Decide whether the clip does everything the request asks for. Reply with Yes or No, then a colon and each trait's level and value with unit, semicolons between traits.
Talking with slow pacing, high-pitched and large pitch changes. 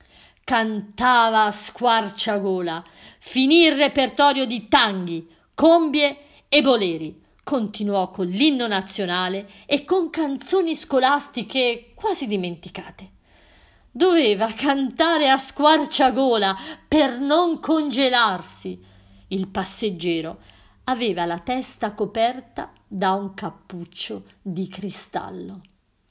Yes: slow, 90 wpm; high, 225 Hz; wide, 6.8 semitones